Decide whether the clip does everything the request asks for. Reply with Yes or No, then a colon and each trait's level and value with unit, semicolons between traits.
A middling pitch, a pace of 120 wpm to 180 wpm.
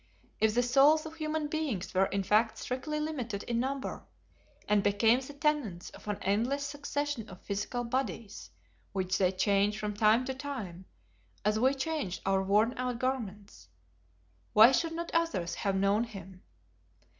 No: high, 230 Hz; average, 155 wpm